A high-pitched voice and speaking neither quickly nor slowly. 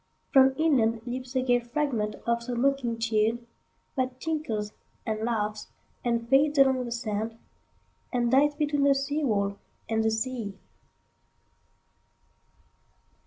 No: high, 240 Hz; slow, 110 wpm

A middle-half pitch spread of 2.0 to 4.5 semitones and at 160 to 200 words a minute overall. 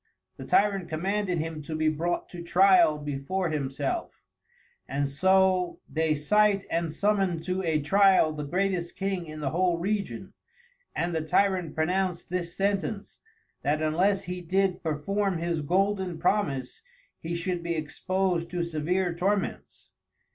No: average, 3.4 semitones; average, 140 wpm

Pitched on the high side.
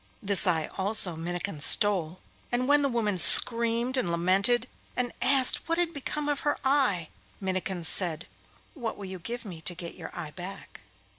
Yes: high, 200 Hz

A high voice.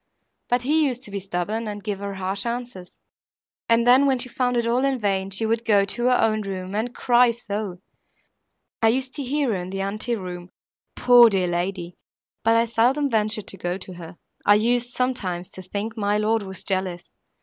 Yes: high, 215 Hz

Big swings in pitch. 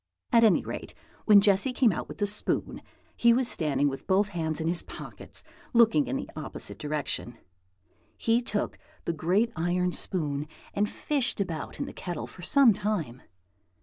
Yes: wide, 6.1 semitones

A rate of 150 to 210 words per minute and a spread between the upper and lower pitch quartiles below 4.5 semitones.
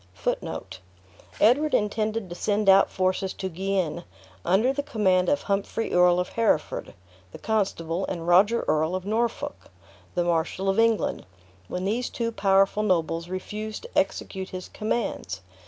No: average, 140 wpm; average, 3.3 semitones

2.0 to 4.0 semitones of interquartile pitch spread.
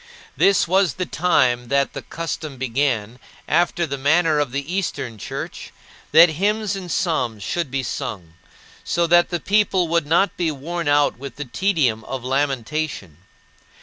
No: average, 4.8 semitones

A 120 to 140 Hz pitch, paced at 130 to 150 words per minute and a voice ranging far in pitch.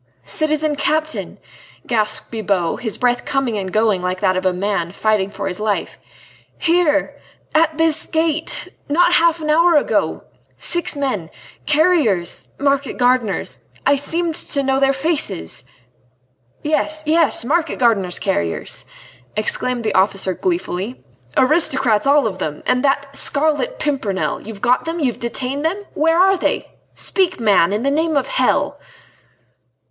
No: very high, 270 Hz; average, 145 wpm; wide, 7.0 semitones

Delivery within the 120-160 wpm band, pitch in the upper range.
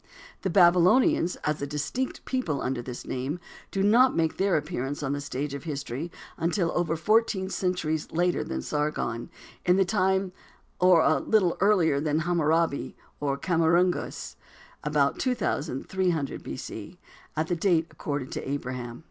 No: average, 150 wpm; medium, 160 Hz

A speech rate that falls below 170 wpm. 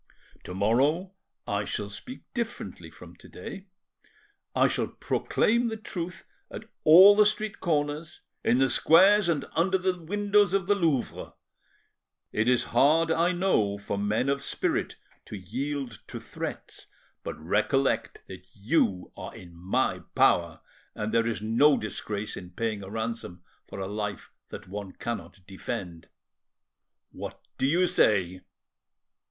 Yes: average, 145 wpm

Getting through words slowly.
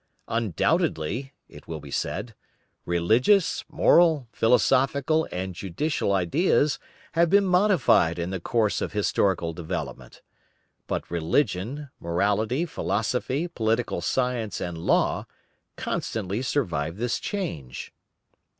Yes: slow, 105 wpm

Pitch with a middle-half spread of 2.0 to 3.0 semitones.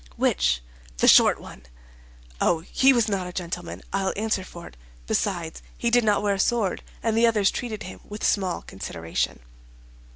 No: average, 4.2 semitones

